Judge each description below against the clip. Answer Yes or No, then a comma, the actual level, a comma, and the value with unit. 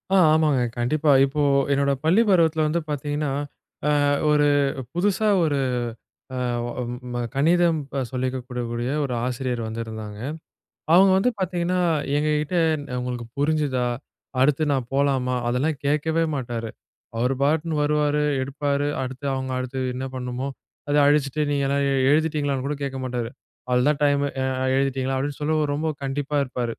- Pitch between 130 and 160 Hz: Yes, medium, 140 Hz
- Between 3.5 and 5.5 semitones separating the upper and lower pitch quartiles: No, average, 3.0 semitones